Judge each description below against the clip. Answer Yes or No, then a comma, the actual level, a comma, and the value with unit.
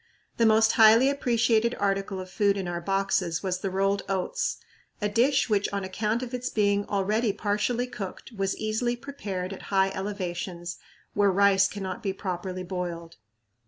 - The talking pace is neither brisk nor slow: Yes, average, 160 wpm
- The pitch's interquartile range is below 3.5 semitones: Yes, average, 2.7 semitones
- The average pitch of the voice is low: No, high, 200 Hz